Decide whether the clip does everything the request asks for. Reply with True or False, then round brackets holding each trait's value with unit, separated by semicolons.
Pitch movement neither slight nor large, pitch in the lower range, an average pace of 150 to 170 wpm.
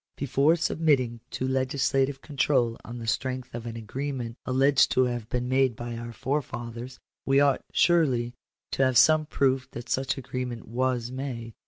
False (2.3 semitones; 130 Hz; 160 wpm)